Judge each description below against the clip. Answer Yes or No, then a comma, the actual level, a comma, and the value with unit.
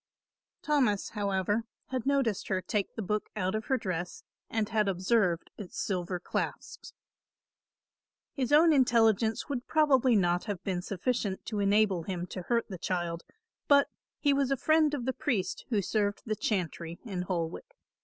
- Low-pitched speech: No, high, 210 Hz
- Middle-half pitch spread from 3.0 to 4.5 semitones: No, average, 5.2 semitones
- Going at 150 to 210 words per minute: Yes, average, 160 wpm